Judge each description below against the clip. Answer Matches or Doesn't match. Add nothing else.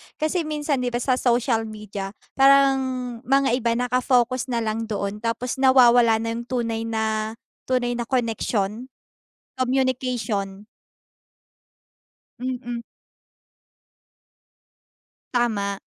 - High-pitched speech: Matches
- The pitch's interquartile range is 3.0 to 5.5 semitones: Doesn't match